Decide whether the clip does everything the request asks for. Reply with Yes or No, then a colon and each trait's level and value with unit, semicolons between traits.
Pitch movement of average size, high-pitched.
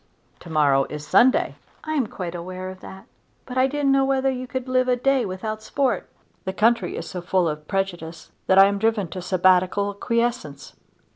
No: wide, 5.9 semitones; high, 200 Hz